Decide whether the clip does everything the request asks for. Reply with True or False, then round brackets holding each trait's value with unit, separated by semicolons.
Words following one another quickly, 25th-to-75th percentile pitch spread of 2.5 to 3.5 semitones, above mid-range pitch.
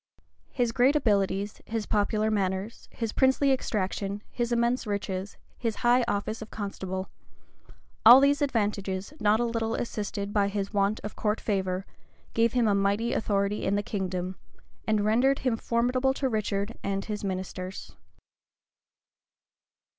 False (140 wpm; 2.9 semitones; 210 Hz)